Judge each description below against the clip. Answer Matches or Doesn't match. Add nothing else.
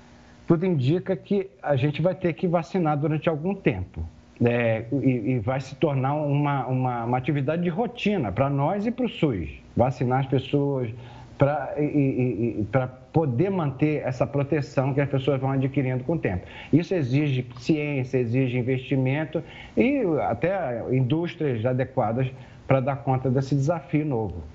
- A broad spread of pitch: Doesn't match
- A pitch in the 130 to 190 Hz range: Matches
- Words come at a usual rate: Matches